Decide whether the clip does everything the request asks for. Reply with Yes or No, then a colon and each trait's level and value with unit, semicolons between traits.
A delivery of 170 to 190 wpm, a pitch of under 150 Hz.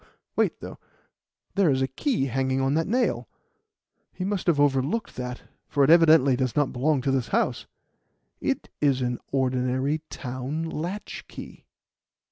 No: average, 145 wpm; low, 135 Hz